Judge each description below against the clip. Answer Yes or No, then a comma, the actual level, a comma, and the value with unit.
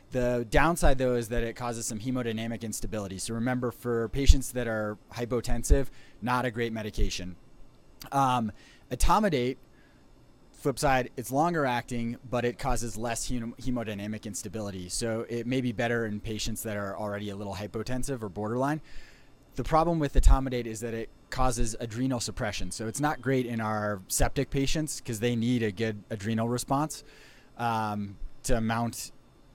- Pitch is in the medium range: No, low, 120 Hz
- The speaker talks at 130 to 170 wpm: Yes, average, 160 wpm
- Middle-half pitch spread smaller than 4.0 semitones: Yes, average, 2.7 semitones